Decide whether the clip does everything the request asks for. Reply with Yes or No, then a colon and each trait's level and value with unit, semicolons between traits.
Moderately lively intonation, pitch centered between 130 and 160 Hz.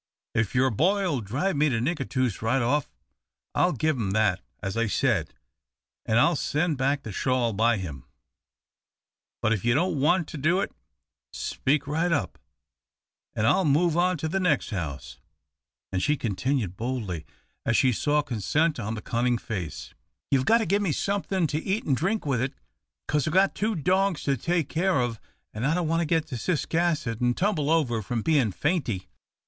No: wide, 6.4 semitones; medium, 140 Hz